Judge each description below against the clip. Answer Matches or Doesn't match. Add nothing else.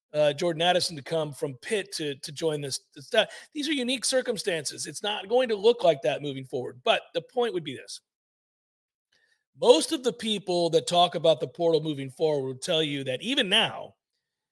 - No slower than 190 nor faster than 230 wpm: Matches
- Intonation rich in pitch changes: Matches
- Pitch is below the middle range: Doesn't match